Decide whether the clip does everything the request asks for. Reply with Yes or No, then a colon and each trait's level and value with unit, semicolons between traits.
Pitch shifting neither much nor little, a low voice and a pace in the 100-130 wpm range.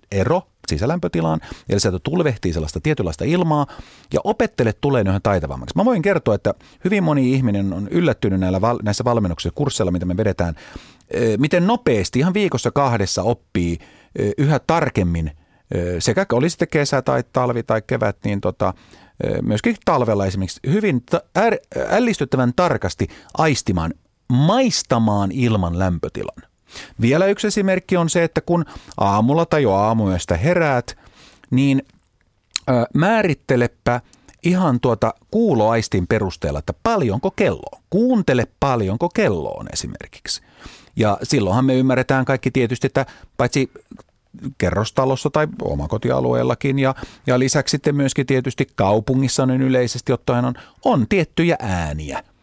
No: wide, 7.2 semitones; low, 125 Hz; average, 125 wpm